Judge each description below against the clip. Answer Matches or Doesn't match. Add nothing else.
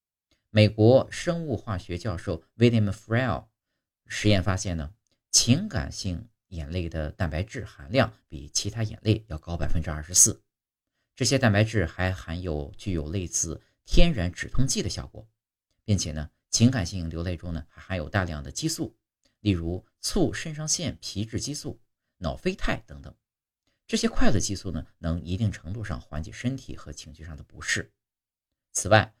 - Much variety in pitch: Doesn't match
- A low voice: Matches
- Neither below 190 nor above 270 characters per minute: Matches